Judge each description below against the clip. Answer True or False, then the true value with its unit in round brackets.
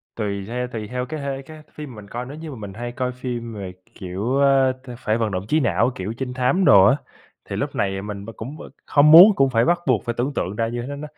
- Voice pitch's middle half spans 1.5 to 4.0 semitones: False (4.4 semitones)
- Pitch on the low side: True (125 Hz)